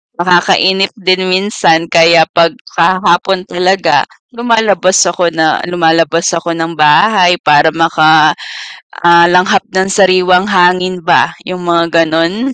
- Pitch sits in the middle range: Yes, medium, 175 Hz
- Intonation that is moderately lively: No, narrow, 2.1 semitones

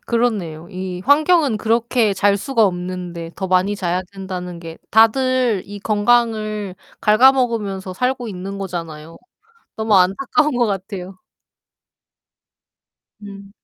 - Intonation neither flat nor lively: Yes, average, 4.2 semitones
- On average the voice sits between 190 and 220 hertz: Yes, high, 200 Hz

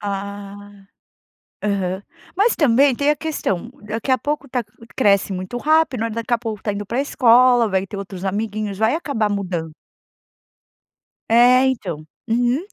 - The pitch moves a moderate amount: Yes, average, 4.2 semitones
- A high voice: Yes, high, 225 Hz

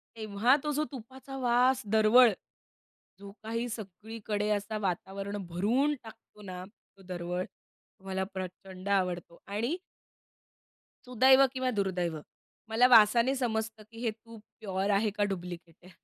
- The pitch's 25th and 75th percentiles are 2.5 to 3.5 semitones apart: No, average, 3.9 semitones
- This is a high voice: Yes, high, 215 Hz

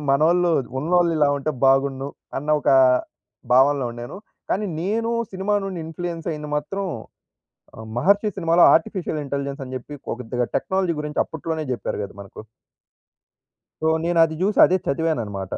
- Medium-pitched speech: Yes, medium, 155 Hz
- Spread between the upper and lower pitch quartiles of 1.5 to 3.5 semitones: No, average, 4.4 semitones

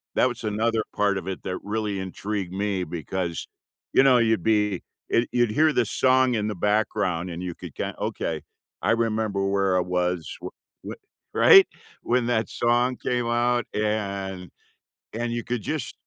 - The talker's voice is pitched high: No, low, 105 Hz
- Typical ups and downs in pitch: Yes, average, 3.7 semitones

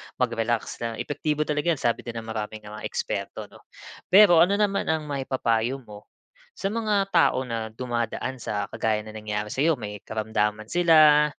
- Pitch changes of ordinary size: No, wide, 5.9 semitones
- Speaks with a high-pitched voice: No, low, 120 Hz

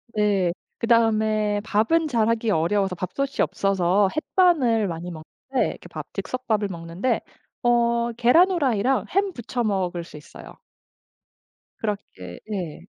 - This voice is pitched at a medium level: No, high, 215 Hz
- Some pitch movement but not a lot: Yes, average, 4.6 semitones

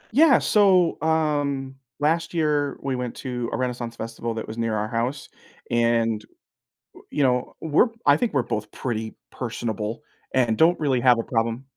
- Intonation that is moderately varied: Yes, average, 4.4 semitones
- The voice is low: Yes, low, 125 Hz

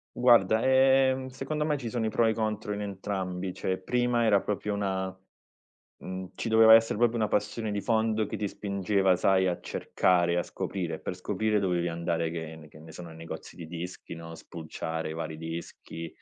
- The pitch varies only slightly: No, average, 4.4 semitones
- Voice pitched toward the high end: No, low, 100 Hz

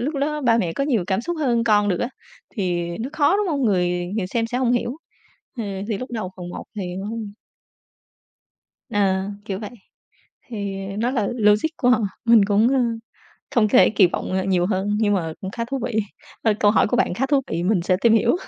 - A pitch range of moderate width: Yes, average, 4.2 semitones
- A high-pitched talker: Yes, high, 215 Hz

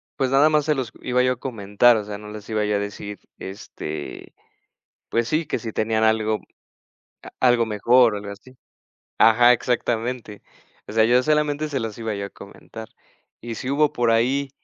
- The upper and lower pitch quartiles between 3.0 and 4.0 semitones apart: Yes, average, 3.3 semitones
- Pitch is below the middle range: Yes, low, 115 Hz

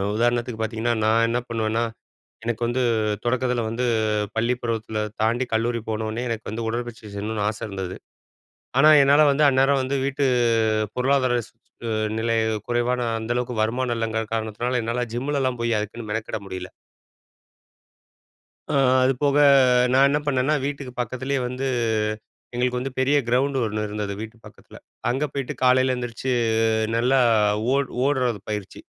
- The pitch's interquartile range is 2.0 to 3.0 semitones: Yes, narrow, 2.6 semitones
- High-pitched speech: No, low, 120 Hz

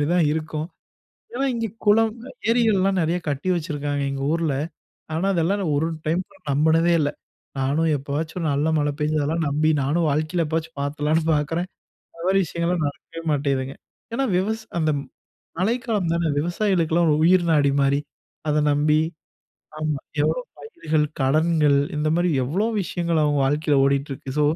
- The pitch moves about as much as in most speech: Yes, average, 3.0 semitones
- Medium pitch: Yes, medium, 160 Hz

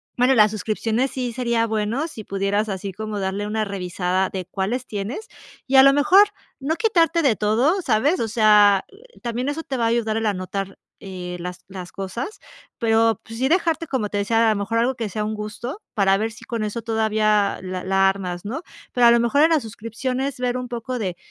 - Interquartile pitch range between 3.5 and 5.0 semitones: Yes, average, 3.9 semitones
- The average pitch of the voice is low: No, high, 220 Hz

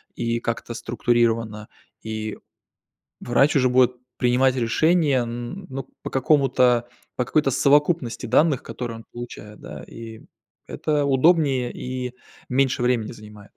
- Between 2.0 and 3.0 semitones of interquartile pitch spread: Yes, average, 2.7 semitones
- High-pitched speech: No, low, 125 Hz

